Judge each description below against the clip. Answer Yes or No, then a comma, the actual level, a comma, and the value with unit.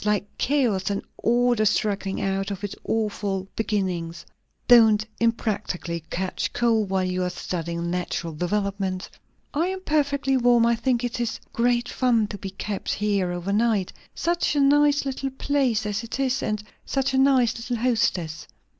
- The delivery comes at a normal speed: Yes, average, 160 wpm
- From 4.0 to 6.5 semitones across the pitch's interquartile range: Yes, average, 4.3 semitones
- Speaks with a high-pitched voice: Yes, high, 215 Hz